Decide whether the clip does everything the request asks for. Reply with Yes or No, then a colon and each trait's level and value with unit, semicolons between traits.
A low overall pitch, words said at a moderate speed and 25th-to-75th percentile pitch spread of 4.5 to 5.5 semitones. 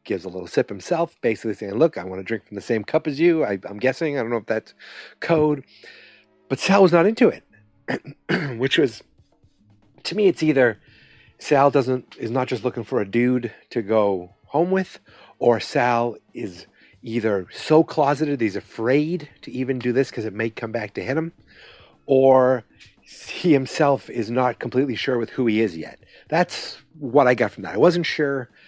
Yes: low, 130 Hz; average, 195 wpm; average, 5.0 semitones